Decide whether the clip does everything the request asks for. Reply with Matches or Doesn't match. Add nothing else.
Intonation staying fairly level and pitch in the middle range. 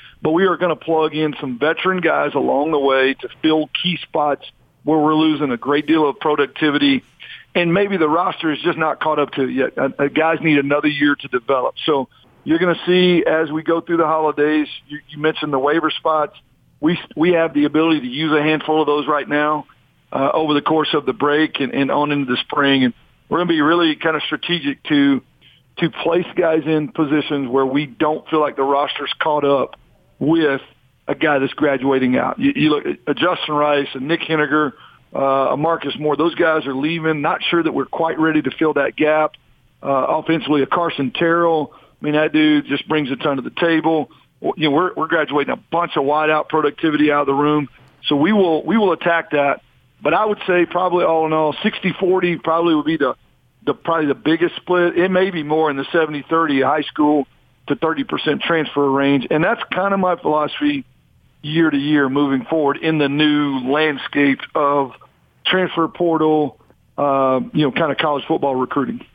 Matches